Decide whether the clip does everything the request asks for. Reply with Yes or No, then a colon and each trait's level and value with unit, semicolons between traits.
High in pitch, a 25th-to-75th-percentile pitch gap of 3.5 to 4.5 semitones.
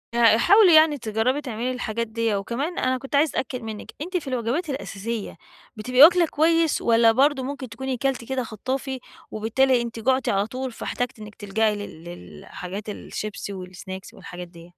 Yes: high, 235 Hz; average, 4.0 semitones